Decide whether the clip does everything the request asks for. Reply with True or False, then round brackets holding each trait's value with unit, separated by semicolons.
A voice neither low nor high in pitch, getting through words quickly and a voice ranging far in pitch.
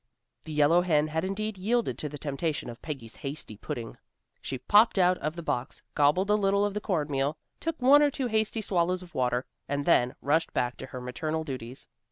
True (160 Hz; 210 wpm; 6.3 semitones)